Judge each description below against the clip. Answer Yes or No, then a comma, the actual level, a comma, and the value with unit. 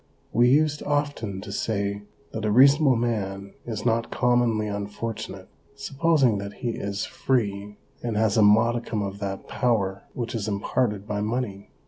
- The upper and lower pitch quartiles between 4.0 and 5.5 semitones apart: No, average, 3.3 semitones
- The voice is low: Yes, low, 110 Hz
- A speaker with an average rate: Yes, average, 160 wpm